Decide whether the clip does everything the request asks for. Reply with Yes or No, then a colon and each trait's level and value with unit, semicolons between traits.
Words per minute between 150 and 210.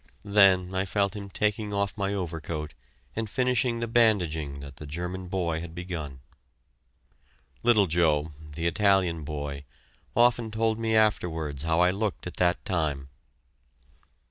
No: average, 140 wpm